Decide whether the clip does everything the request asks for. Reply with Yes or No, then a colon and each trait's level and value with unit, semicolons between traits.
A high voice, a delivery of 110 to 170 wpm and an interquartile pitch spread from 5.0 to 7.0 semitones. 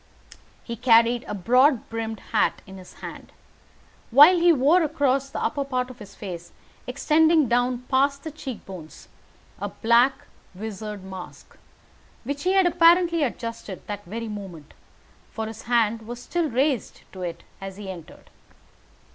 Yes: high, 240 Hz; average, 150 wpm; average, 5.3 semitones